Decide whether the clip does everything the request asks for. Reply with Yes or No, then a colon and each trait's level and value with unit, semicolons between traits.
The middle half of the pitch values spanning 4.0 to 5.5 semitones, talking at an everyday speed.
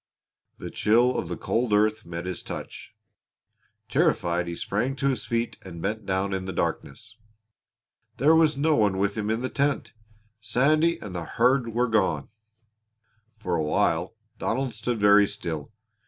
Yes: average, 4.9 semitones; average, 160 wpm